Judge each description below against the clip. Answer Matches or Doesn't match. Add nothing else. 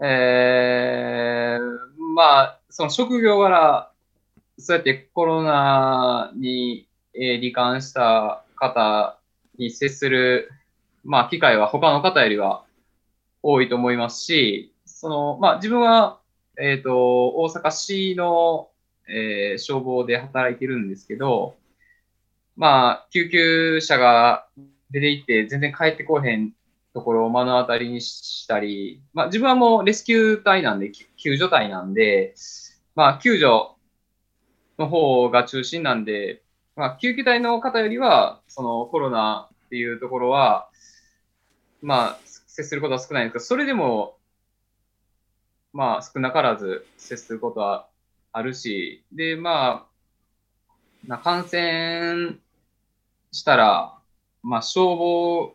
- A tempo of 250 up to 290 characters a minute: Doesn't match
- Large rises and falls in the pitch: Matches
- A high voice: Doesn't match